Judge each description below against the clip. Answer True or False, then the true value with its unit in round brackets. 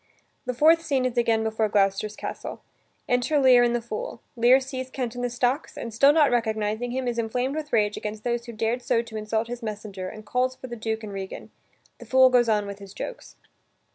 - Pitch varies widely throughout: False (2.8 semitones)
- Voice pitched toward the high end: True (235 Hz)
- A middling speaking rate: False (220 wpm)